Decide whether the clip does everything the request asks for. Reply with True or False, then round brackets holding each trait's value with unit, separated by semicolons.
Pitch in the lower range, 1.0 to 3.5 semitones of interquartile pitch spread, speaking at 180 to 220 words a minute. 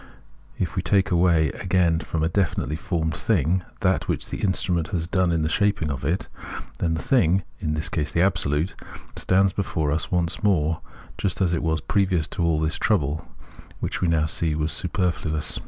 True (85 Hz; 2.9 semitones; 190 wpm)